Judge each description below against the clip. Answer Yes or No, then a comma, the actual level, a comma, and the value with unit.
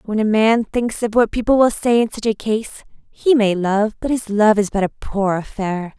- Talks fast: Yes, fast, 240 wpm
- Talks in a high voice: Yes, high, 215 Hz